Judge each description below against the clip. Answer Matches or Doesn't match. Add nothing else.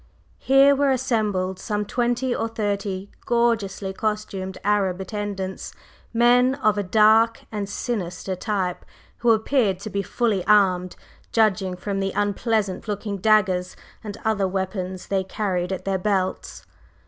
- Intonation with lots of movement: Doesn't match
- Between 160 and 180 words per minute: Doesn't match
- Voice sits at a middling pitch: Doesn't match